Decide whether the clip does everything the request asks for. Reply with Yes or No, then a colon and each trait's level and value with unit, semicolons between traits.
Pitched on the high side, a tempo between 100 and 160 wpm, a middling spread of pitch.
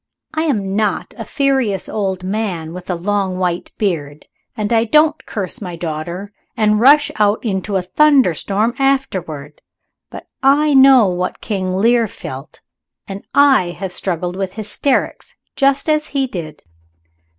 No: high, 205 Hz; average, 145 wpm; wide, 6.6 semitones